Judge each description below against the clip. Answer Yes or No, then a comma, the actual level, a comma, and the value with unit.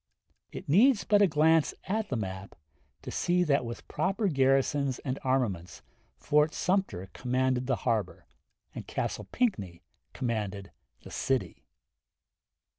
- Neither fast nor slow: No, slow, 125 wpm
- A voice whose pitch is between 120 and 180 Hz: Yes, low, 135 Hz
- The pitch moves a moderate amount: No, wide, 7.1 semitones